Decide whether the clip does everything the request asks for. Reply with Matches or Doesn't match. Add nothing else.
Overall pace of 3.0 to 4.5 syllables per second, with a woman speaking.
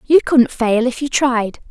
Matches